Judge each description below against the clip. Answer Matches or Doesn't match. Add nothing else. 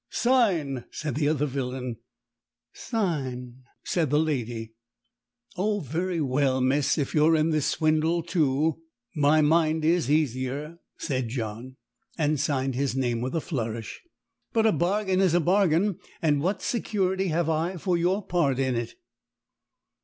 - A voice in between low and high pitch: Matches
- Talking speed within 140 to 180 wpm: Matches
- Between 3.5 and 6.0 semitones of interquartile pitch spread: Matches